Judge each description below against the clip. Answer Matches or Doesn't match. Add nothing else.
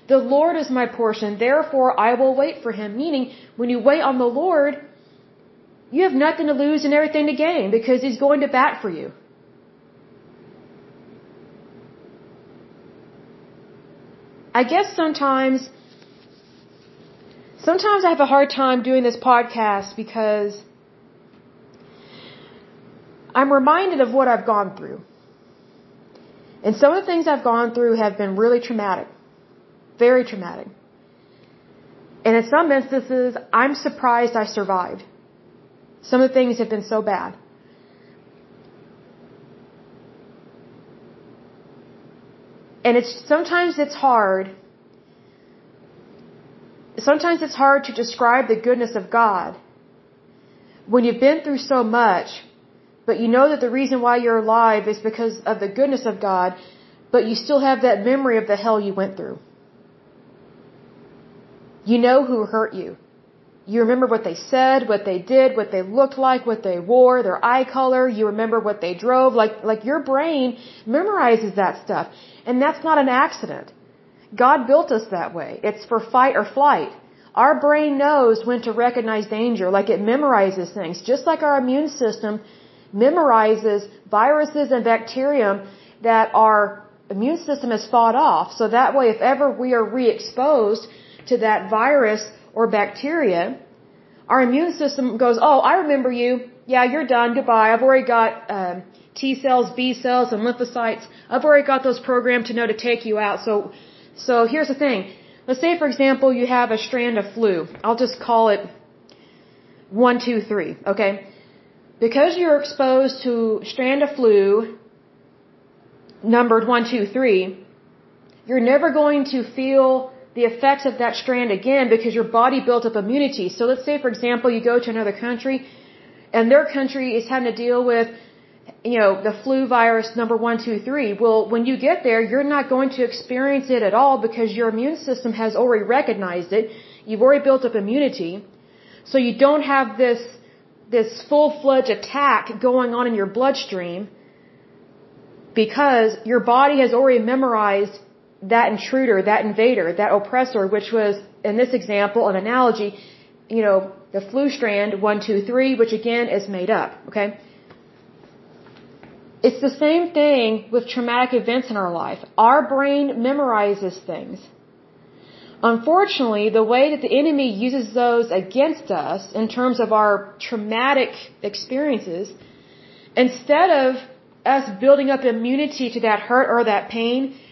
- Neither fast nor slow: Matches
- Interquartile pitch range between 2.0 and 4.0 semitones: Matches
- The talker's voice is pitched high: Matches